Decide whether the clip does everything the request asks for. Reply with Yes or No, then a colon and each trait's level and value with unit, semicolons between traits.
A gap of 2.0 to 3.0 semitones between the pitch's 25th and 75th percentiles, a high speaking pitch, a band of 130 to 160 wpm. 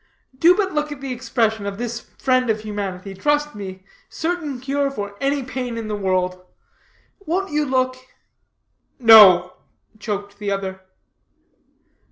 No: wide, 5.5 semitones; high, 235 Hz; average, 140 wpm